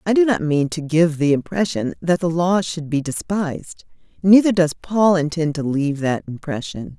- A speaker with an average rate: Yes, average, 190 wpm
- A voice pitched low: No, medium, 165 Hz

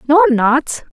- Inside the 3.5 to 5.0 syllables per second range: Yes, 4.5 syllables/s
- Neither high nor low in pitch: No, very high, 290 Hz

